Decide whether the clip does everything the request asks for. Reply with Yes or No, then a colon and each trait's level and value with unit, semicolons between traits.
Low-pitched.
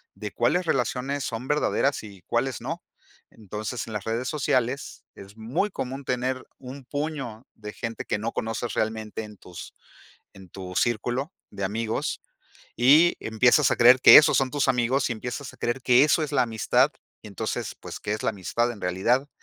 Yes: low, 120 Hz